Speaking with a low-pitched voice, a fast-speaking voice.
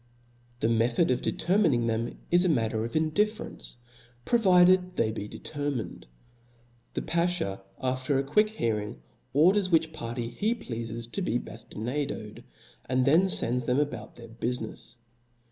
No: low, 130 Hz; slow, 135 wpm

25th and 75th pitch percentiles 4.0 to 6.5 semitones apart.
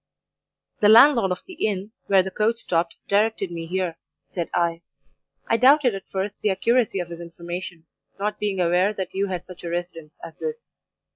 No: average, 3.5 semitones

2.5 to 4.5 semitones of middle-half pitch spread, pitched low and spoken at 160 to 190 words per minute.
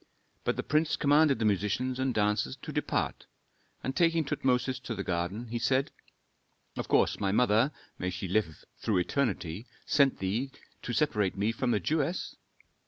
No: average, 5.1 semitones; low, 120 Hz; average, 165 wpm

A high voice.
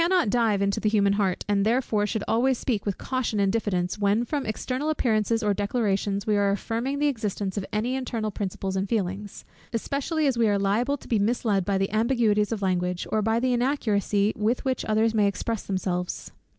Yes: high, 215 Hz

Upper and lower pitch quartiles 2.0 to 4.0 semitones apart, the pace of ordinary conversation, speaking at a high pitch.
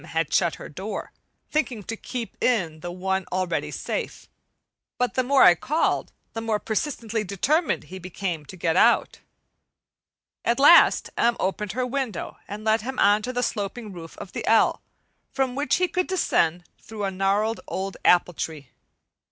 No: wide, 5.4 semitones; average, 170 wpm; high, 210 Hz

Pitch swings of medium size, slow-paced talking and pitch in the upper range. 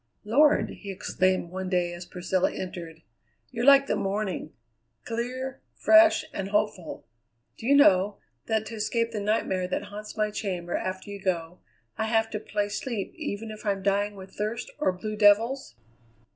No: average, 3.1 semitones; average, 165 wpm; high, 205 Hz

